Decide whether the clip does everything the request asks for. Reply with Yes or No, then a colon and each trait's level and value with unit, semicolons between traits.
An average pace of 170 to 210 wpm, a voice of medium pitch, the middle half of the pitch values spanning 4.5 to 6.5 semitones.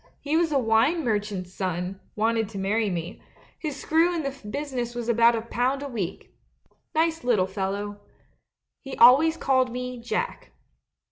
No: average, 175 wpm; high, 235 Hz; average, 5.2 semitones